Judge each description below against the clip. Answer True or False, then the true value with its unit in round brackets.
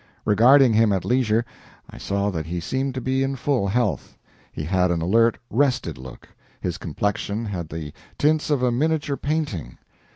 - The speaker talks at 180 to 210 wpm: False (170 wpm)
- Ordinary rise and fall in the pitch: False (6.5 semitones)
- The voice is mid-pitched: False (115 Hz)